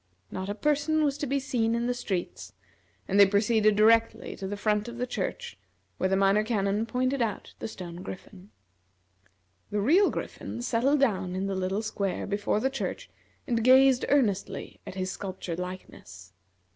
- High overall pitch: Yes, high, 215 Hz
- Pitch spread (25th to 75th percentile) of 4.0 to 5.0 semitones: Yes, average, 4.4 semitones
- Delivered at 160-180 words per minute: Yes, average, 170 wpm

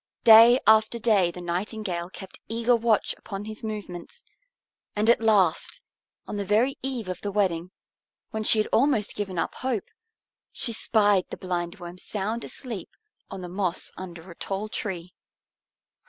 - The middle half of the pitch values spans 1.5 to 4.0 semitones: Yes, average, 3.5 semitones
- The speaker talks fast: No, average, 155 wpm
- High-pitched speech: Yes, high, 205 Hz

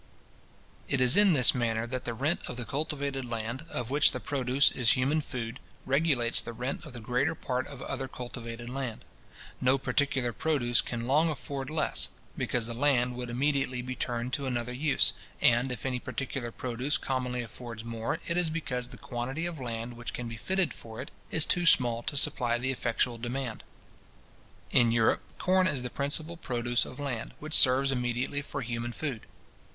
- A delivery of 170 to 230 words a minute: Yes, average, 185 wpm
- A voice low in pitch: Yes, low, 125 Hz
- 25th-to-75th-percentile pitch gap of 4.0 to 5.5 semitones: No, average, 2.8 semitones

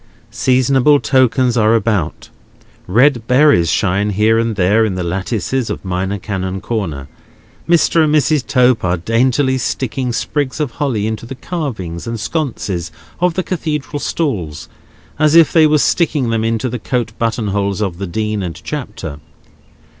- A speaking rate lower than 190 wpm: Yes, average, 155 wpm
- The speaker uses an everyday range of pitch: No, wide, 5.7 semitones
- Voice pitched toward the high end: No, low, 115 Hz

